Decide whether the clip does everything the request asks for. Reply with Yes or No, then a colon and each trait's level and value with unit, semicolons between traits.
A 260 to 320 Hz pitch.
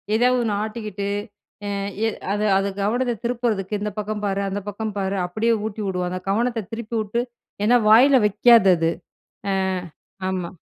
No: high, 215 Hz